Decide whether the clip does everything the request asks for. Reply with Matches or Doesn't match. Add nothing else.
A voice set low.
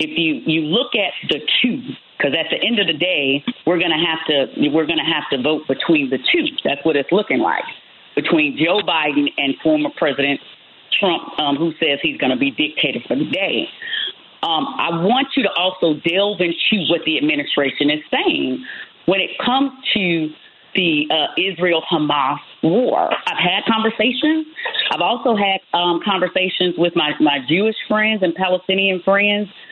Doesn't match